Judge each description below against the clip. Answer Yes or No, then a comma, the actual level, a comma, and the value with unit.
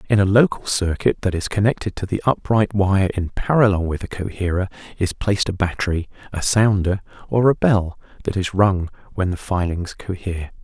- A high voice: No, very low, 95 Hz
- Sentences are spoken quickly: No, average, 180 wpm